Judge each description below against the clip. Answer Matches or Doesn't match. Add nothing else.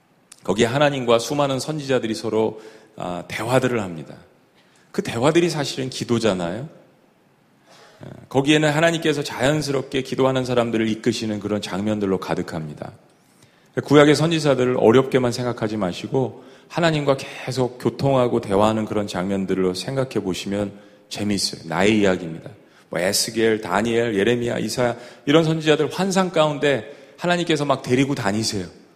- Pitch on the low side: Matches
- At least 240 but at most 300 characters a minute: Doesn't match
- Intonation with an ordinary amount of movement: Matches